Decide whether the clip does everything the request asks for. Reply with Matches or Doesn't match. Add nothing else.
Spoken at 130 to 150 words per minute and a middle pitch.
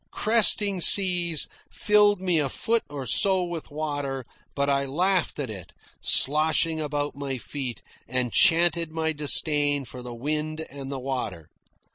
Matches